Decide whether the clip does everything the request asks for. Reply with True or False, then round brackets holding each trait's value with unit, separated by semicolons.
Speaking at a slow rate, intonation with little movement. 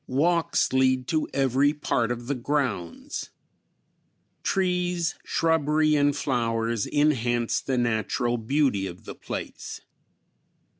False (105 wpm; 4.2 semitones)